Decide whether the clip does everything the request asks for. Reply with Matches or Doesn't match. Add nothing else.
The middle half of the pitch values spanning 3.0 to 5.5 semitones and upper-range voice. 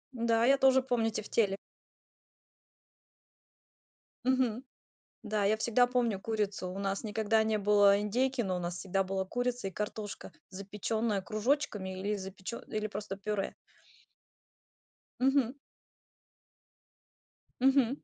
Matches